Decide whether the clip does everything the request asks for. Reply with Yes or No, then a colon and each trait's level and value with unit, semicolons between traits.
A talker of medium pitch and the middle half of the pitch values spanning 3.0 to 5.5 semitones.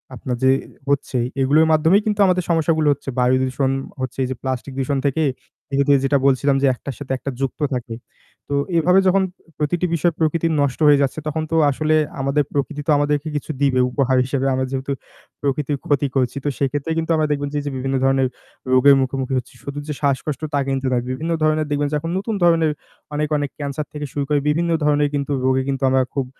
No: medium, 145 Hz; narrow, 2.5 semitones